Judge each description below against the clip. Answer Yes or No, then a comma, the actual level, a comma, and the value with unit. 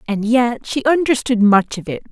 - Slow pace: No, average, 200 wpm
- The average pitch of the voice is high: Yes, high, 235 Hz